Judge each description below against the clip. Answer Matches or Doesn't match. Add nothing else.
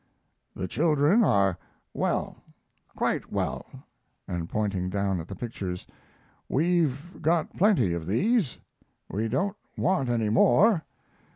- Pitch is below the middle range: Matches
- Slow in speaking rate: Matches